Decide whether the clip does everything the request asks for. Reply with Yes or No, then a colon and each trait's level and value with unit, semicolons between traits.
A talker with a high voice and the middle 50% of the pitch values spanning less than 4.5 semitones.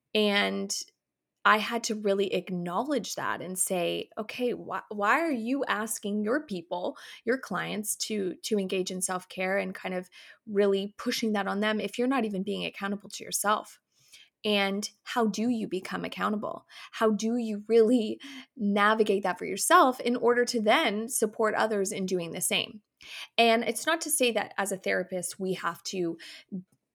Yes: high, 210 Hz; average, 3.4 semitones